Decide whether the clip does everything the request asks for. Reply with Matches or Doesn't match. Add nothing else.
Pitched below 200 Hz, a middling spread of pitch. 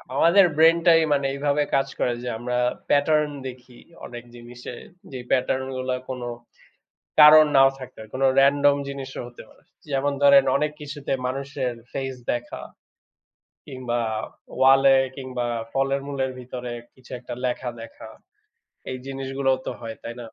Doesn't match